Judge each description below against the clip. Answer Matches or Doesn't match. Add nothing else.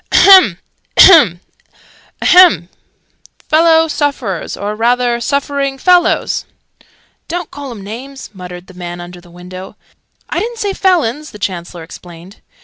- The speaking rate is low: Matches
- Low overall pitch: Doesn't match